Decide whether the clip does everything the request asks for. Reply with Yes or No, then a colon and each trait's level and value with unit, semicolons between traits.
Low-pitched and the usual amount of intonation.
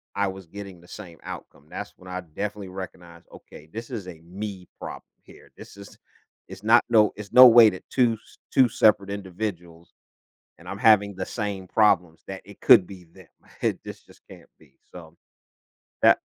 Yes: very low, 95 Hz; average, 3.1 semitones